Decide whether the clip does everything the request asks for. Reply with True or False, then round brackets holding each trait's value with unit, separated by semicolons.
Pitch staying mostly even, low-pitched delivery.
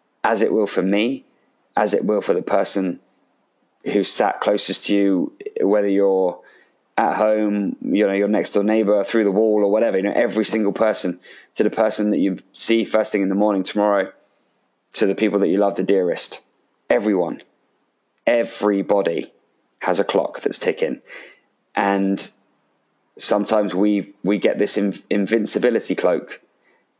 True (1.6 semitones; 105 Hz)